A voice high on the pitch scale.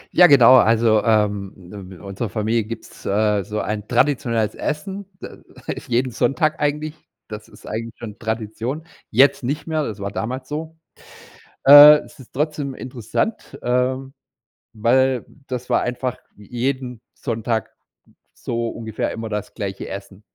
No: low, 120 Hz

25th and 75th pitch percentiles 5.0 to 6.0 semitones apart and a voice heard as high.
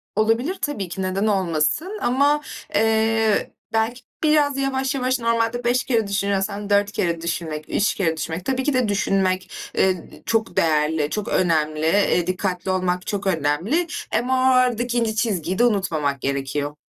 Yes: wide, 5.6 semitones; high, 205 Hz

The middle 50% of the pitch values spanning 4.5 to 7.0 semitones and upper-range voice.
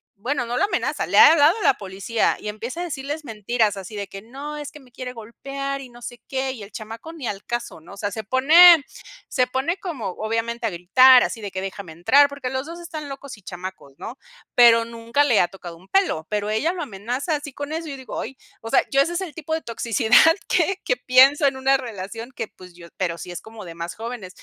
Yes: average, 5.3 semitones; high, 245 Hz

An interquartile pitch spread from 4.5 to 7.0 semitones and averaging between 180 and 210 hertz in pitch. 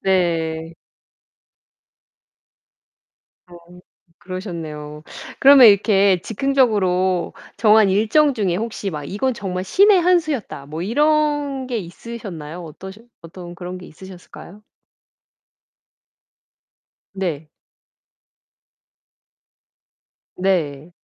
Yes: average, 5.3 semitones; high, 190 Hz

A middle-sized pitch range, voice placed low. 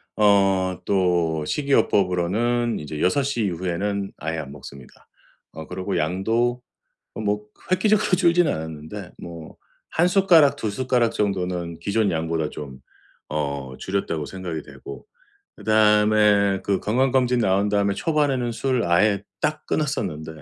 No: wide, 6.1 semitones; low, 100 Hz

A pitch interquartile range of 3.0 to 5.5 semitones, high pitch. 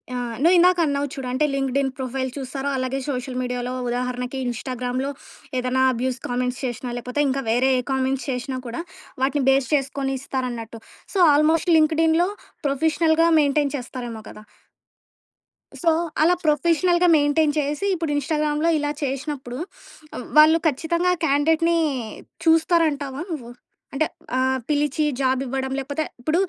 Yes: average, 3.4 semitones; very high, 275 Hz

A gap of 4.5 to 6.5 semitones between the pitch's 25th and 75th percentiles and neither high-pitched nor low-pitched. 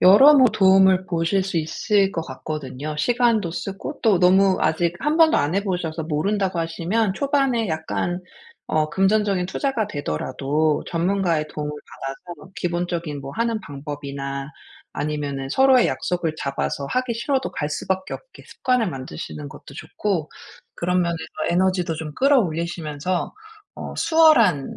Yes: average, 5.2 semitones; medium, 175 Hz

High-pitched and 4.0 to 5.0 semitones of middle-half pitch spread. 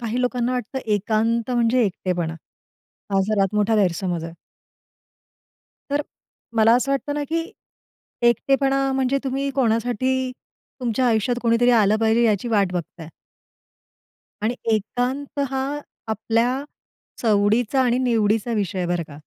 No: high, 230 Hz; average, 3.5 semitones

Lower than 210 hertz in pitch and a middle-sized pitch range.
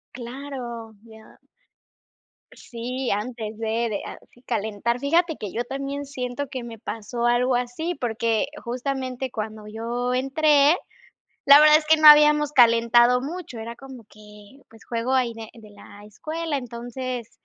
No: high, 245 Hz; average, 3.3 semitones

